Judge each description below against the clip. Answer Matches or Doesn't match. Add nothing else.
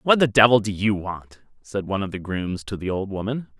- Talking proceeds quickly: Matches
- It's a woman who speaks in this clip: Doesn't match